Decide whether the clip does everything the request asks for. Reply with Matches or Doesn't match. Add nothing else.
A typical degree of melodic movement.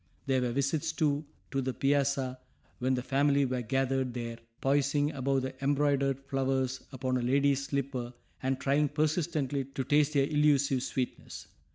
Doesn't match